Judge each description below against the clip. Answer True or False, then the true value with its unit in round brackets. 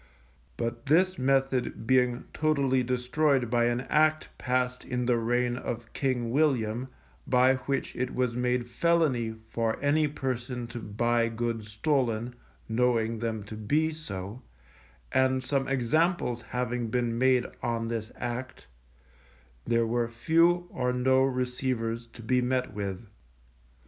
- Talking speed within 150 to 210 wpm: False (135 wpm)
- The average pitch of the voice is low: True (125 Hz)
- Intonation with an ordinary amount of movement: False (2.1 semitones)